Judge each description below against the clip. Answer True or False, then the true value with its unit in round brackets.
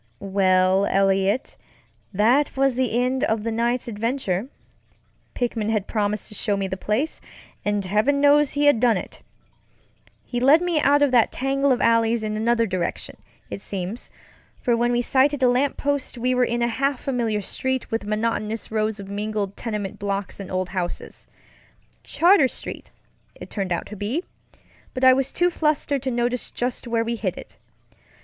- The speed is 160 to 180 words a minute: True (175 wpm)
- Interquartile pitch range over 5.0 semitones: False (4.2 semitones)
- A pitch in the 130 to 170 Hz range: False (230 Hz)